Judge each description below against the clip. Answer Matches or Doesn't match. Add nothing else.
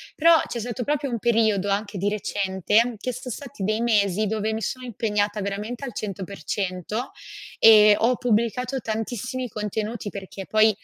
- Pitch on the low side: Doesn't match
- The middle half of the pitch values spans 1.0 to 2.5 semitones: Doesn't match